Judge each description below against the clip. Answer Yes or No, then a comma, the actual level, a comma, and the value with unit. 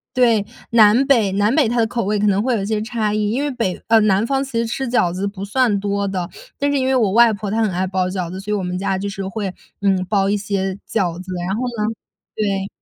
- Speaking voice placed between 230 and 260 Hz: No, high, 210 Hz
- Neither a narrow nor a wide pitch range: Yes, average, 3.1 semitones